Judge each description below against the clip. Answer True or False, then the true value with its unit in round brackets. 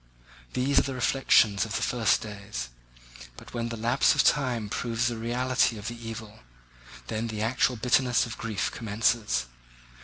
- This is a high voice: False (115 Hz)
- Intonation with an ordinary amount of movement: False (2.2 semitones)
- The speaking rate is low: False (160 wpm)